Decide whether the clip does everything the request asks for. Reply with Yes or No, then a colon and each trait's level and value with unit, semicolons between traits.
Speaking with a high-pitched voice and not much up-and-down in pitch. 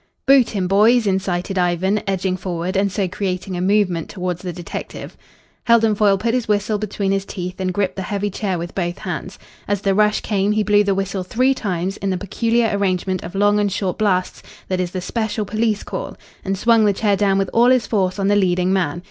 Yes: high, 195 Hz; narrow, 2.3 semitones